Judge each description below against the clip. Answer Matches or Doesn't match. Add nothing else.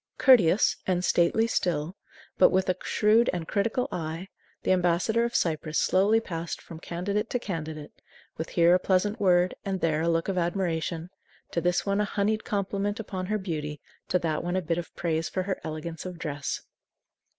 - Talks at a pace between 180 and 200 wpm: Matches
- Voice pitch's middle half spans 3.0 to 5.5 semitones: Matches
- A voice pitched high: Doesn't match